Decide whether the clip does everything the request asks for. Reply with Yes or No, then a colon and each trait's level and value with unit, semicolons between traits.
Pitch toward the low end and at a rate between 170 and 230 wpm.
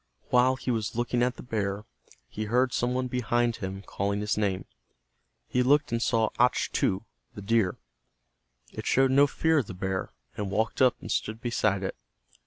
Yes: low, 115 Hz; average, 180 wpm